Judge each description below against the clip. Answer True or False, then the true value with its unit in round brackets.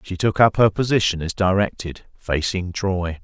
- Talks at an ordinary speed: True (165 wpm)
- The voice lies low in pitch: True (95 Hz)